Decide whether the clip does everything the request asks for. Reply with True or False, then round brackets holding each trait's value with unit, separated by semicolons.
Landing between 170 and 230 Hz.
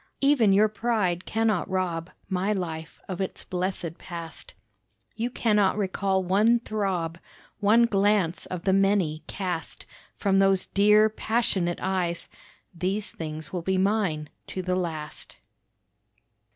True (190 Hz)